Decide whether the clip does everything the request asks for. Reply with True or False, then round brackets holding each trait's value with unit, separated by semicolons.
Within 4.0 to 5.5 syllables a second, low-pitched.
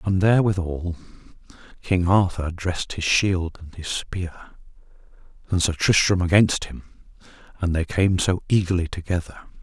True (4.8 syllables/s; 90 Hz)